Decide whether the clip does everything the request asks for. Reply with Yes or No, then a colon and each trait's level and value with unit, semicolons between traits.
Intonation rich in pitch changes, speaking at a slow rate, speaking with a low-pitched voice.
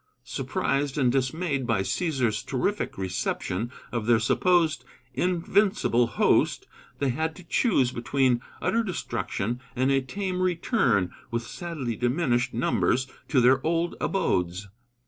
Yes: wide, 6.2 semitones; slow, 125 wpm; low, 130 Hz